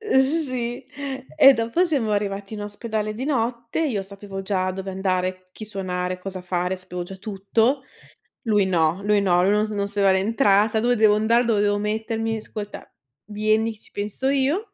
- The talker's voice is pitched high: Yes, high, 210 Hz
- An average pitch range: Yes, average, 3.1 semitones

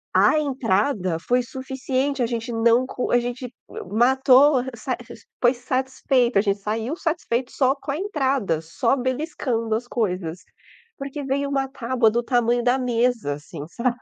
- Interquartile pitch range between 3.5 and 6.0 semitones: No, average, 2.7 semitones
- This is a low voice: No, high, 245 Hz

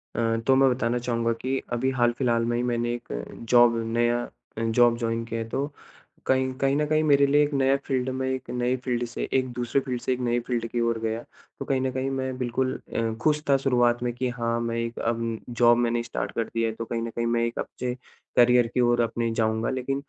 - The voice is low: Yes, low, 120 Hz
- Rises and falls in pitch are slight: Yes, narrow, 2.0 semitones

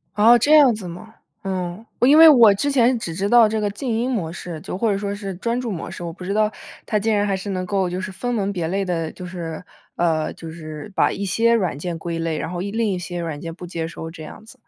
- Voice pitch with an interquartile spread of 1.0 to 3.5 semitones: No, average, 4.5 semitones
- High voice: Yes, high, 195 Hz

